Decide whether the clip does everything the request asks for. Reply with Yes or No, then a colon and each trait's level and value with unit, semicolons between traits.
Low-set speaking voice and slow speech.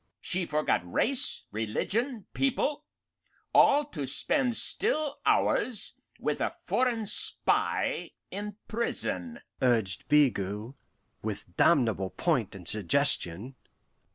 No: medium, 155 Hz; slow, 100 wpm